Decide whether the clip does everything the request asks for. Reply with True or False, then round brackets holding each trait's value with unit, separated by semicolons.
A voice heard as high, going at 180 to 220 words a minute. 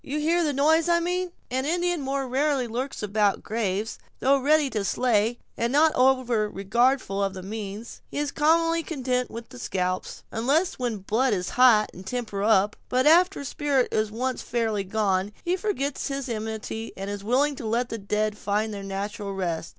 True (240 Hz; 190 wpm)